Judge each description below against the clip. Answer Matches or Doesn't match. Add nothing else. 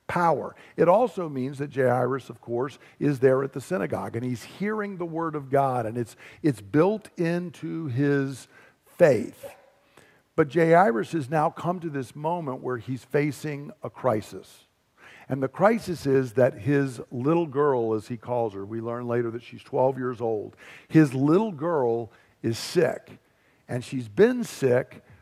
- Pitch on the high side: Doesn't match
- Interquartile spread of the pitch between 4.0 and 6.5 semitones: Matches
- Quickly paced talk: Doesn't match